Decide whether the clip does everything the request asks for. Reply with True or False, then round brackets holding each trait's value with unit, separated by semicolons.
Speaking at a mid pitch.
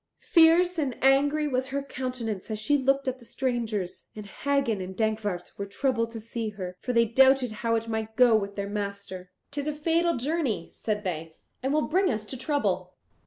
False (235 Hz)